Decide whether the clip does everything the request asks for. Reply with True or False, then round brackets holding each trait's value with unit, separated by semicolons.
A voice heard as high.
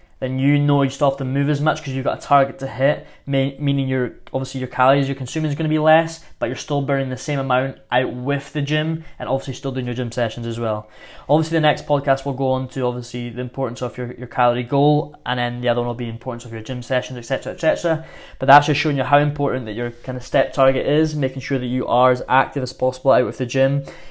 False (135 Hz)